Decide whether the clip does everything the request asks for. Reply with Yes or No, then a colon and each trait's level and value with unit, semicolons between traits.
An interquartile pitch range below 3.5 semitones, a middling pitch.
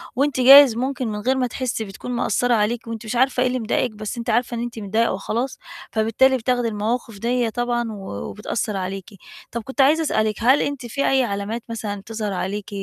No: average, 2.9 semitones; high, 235 Hz